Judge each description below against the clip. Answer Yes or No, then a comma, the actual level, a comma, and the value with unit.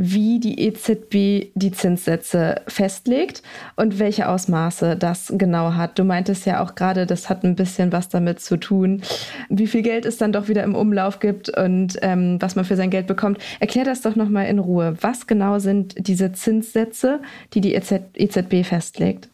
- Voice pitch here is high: Yes, high, 195 Hz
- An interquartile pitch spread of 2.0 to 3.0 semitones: Yes, average, 2.7 semitones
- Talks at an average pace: Yes, average, 180 wpm